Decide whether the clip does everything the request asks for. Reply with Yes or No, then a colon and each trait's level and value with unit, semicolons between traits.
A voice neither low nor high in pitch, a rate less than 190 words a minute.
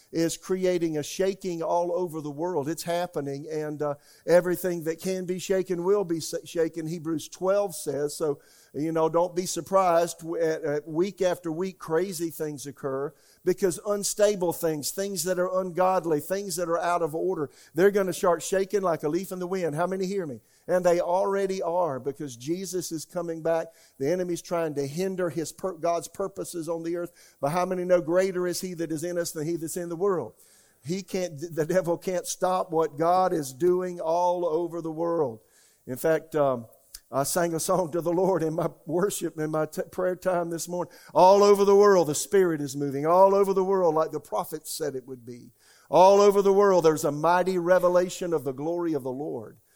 No: medium, 175 Hz; fast, 205 wpm